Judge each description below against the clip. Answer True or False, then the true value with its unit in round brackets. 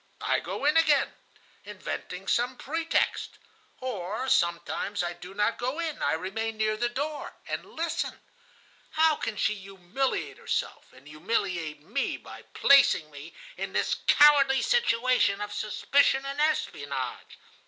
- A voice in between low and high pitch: False (230 Hz)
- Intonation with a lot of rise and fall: True (7.0 semitones)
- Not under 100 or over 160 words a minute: True (135 wpm)